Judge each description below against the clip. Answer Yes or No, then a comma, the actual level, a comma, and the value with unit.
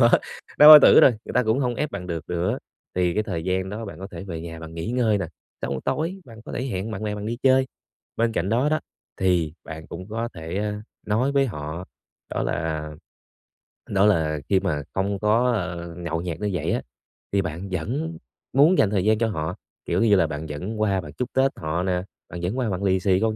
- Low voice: Yes, low, 100 Hz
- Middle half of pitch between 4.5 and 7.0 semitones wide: Yes, average, 5.0 semitones